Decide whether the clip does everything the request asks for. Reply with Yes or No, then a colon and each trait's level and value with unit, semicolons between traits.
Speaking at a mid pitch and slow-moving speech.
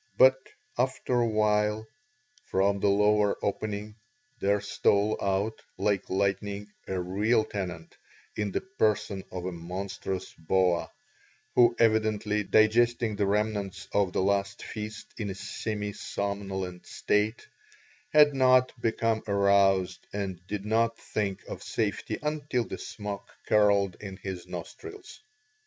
No: low, 105 Hz; slow, 125 wpm